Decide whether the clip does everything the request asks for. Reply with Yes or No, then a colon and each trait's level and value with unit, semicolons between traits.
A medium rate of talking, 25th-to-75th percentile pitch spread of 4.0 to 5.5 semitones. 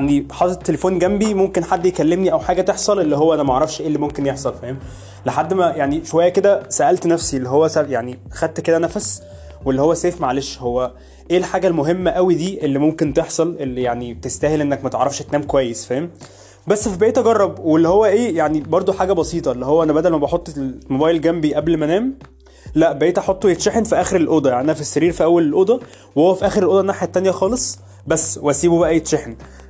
No: fast, 205 wpm; average, 5.0 semitones